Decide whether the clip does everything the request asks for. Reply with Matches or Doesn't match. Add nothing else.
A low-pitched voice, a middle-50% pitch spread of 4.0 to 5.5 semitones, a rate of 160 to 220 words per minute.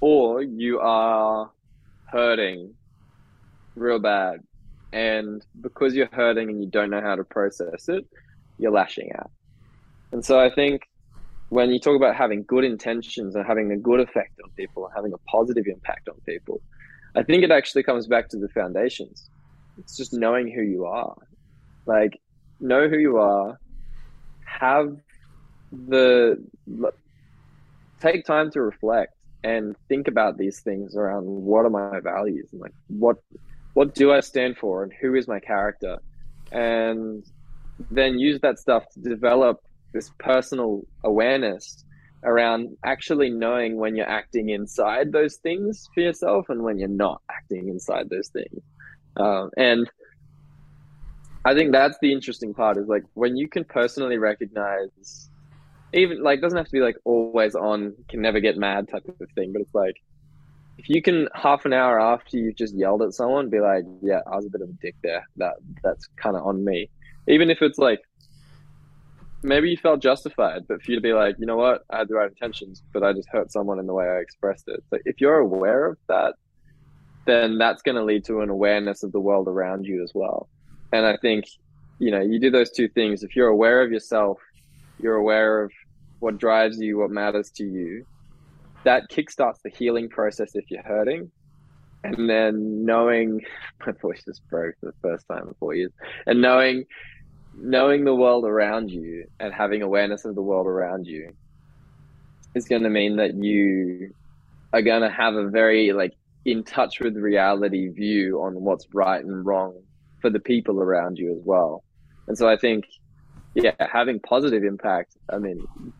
Matches